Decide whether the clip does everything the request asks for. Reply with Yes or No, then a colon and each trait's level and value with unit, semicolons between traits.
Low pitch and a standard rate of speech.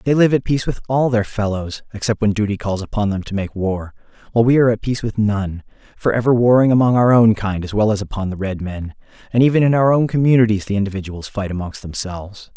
No: low, 110 Hz; fast, 230 wpm